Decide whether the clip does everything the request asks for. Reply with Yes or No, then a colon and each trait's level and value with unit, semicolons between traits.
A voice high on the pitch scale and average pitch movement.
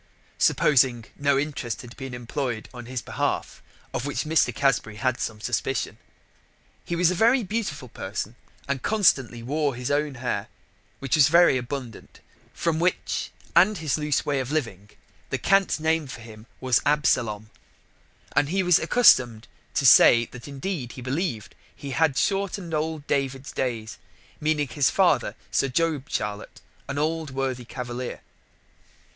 No: low, 135 Hz; average, 4.4 semitones